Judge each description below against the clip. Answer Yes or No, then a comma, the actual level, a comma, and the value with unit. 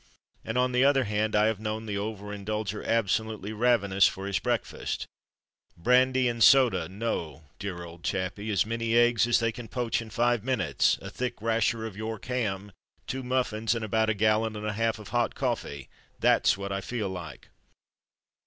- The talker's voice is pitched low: Yes, low, 110 Hz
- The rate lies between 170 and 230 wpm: Yes, average, 180 wpm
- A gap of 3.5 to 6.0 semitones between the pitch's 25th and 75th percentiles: No, average, 2.8 semitones